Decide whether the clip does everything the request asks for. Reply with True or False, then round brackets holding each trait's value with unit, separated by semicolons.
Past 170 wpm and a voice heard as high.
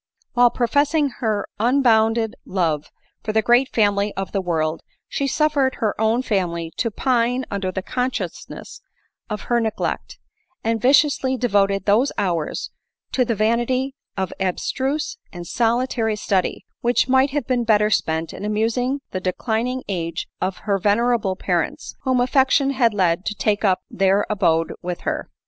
False (150 wpm; 220 Hz)